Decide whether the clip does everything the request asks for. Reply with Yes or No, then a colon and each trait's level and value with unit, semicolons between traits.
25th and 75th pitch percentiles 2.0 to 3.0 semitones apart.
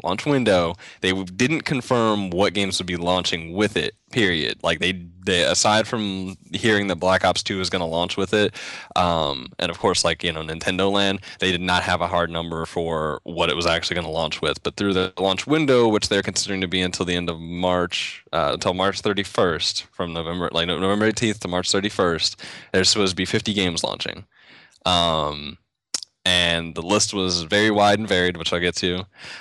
Yes: narrow, 2.5 semitones